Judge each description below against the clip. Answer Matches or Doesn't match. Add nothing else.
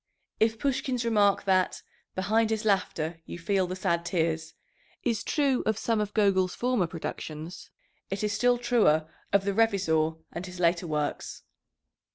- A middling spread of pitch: Matches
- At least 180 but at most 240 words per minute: Doesn't match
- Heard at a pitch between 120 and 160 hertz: Doesn't match